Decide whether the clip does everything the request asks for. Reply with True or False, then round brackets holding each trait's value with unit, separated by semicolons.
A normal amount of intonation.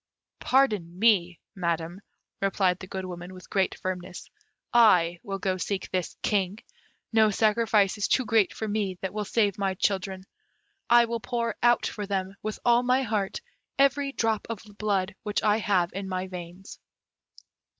True (3.1 semitones)